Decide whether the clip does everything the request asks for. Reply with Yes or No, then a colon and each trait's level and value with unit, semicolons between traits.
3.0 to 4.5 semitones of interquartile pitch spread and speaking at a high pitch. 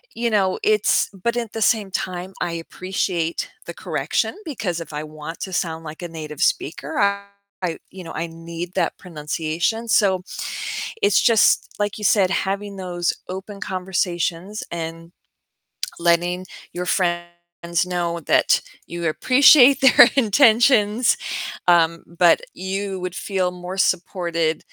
No: average, 3.3 semitones; medium, 180 Hz